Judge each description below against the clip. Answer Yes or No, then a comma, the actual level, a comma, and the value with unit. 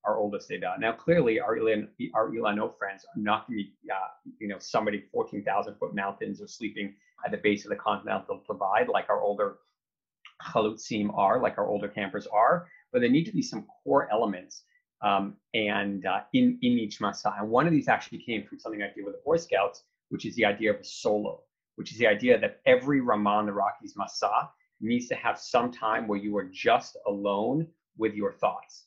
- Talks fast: Yes, fast, 210 wpm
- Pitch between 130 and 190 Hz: No, low, 110 Hz